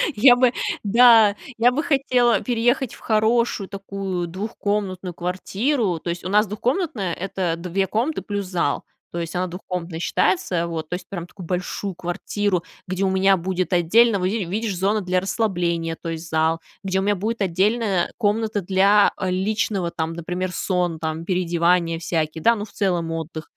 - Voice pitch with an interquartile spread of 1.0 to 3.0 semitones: No, average, 3.4 semitones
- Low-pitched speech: No, high, 190 Hz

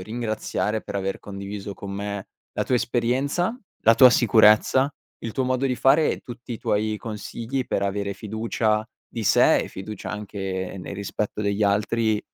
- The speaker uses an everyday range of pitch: Yes, average, 3.0 semitones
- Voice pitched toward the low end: Yes, low, 110 Hz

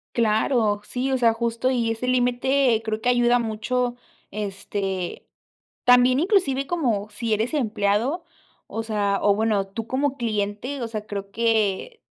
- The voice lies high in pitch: Yes, high, 230 Hz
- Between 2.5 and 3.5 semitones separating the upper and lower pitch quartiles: Yes, average, 3.2 semitones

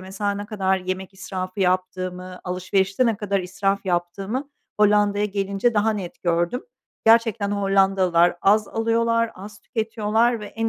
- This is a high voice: Yes, high, 200 Hz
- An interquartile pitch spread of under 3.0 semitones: Yes, narrow, 2.5 semitones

